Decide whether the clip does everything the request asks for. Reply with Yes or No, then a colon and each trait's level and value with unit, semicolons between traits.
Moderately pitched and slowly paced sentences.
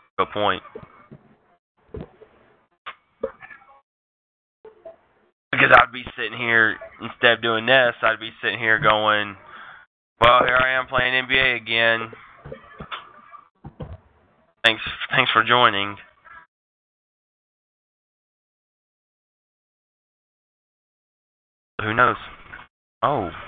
No: low, 115 Hz; slow, 75 wpm